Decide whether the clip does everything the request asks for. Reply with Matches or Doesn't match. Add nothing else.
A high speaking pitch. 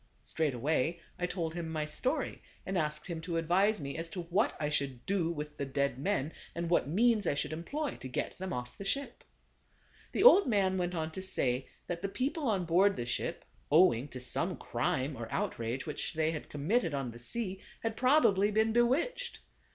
Doesn't match